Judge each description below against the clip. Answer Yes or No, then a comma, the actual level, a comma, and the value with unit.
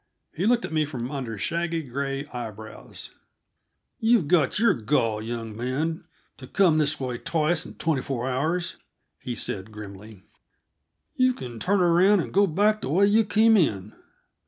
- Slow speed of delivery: No, average, 160 wpm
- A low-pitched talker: No, medium, 150 Hz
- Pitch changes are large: Yes, wide, 7.1 semitones